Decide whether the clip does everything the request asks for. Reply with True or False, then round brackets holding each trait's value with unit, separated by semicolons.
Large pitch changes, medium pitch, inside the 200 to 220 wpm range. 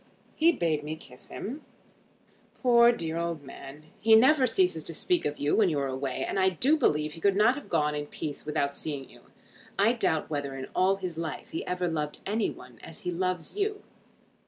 True (6.8 semitones; 170 Hz; 205 wpm)